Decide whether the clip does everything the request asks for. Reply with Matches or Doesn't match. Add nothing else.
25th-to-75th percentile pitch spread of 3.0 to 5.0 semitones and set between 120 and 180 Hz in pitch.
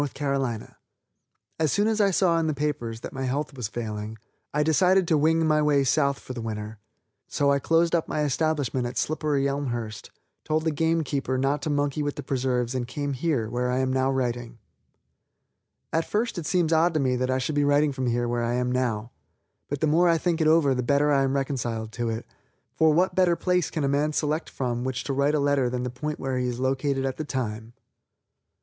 Matches